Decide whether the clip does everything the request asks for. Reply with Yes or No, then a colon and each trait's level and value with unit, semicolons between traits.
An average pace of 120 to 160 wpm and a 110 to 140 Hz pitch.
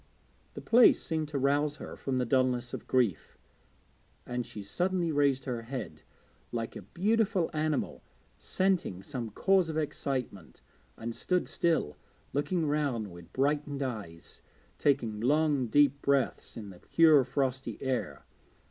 Yes: average, 140 wpm; low, 135 Hz